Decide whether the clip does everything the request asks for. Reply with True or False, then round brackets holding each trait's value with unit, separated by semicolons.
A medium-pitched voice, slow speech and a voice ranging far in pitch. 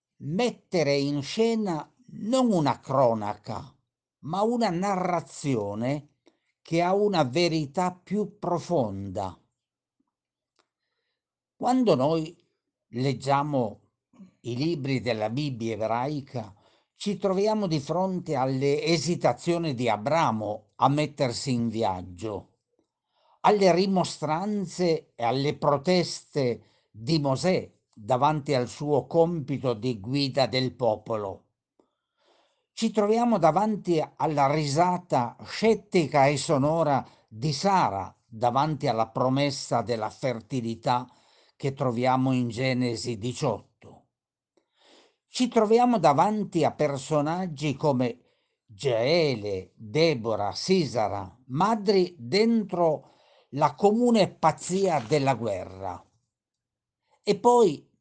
True (145 Hz; 90 wpm; 6.4 semitones)